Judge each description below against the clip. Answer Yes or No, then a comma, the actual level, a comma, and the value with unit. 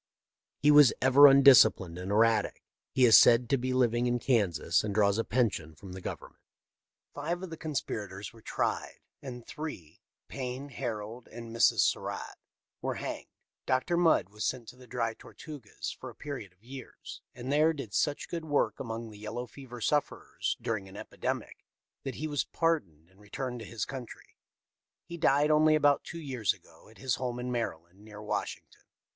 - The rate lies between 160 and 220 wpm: Yes, average, 185 wpm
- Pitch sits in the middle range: No, low, 120 Hz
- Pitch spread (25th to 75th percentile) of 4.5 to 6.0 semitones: Yes, average, 4.8 semitones